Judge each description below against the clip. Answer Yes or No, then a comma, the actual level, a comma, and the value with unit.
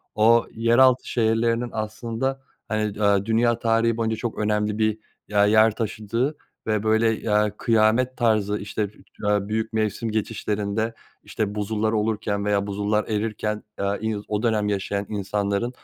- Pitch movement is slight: Yes, narrow, 1.5 semitones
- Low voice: Yes, low, 110 Hz